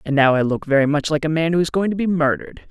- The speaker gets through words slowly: No, fast, 330 wpm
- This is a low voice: No, medium, 155 Hz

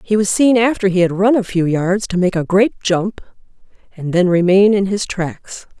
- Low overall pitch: No, high, 190 Hz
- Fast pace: Yes, fast, 215 wpm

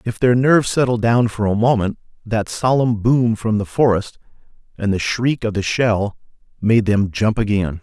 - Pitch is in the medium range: No, low, 110 Hz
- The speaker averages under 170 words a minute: No, average, 185 wpm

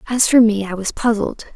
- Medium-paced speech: No, fast, 230 wpm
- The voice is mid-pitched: No, high, 215 Hz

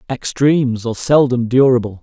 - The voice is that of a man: Yes, male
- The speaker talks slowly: Yes, slow, 120 wpm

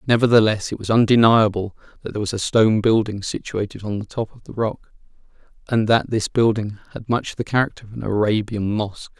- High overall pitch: No, low, 110 Hz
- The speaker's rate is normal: Yes, average, 190 wpm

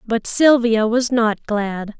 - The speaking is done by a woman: Yes, female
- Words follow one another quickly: No, average, 150 wpm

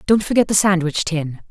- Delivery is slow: No, average, 200 wpm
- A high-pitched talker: No, medium, 180 Hz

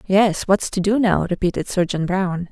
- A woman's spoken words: Yes, female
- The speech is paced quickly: No, average, 190 wpm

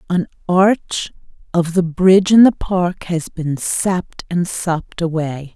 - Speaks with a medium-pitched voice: Yes, medium, 175 Hz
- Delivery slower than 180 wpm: Yes, average, 150 wpm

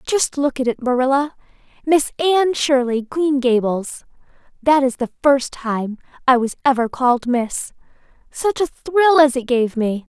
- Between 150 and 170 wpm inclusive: Yes, average, 160 wpm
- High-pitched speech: Yes, very high, 265 Hz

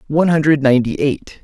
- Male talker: Yes, male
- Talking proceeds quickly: No, average, 170 wpm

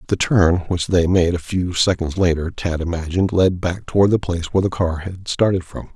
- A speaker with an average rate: No, fast, 220 wpm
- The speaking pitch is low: Yes, very low, 90 Hz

